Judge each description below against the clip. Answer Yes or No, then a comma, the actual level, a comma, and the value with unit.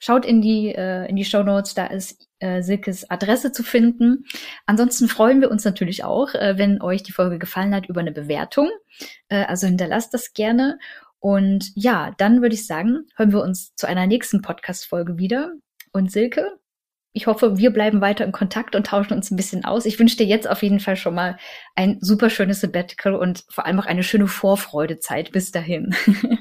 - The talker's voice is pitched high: Yes, high, 200 Hz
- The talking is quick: Yes, fast, 200 wpm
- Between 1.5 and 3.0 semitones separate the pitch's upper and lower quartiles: No, average, 3.6 semitones